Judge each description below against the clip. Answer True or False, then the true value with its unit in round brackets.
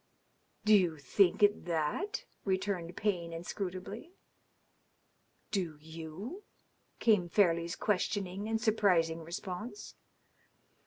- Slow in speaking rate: True (90 wpm)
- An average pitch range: True (3.8 semitones)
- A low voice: False (185 Hz)